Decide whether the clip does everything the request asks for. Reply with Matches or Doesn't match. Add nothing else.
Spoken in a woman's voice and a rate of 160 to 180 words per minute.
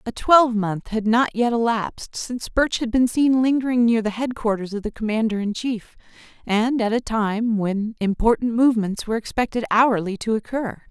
Matches